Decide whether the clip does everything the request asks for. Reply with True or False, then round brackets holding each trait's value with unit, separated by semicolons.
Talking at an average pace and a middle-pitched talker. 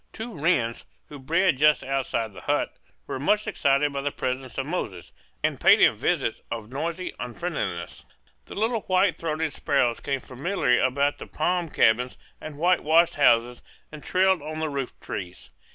True (160 wpm; 145 Hz)